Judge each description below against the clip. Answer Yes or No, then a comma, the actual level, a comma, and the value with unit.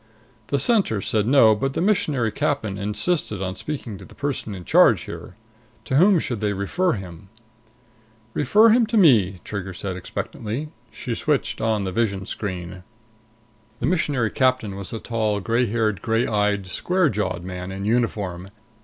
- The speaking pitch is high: No, low, 110 Hz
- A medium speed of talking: Yes, average, 160 wpm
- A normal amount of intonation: No, wide, 5.9 semitones